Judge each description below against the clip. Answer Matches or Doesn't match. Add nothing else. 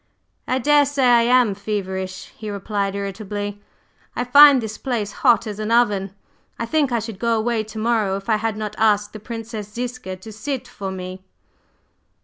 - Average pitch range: Matches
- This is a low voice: Doesn't match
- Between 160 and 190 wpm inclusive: Matches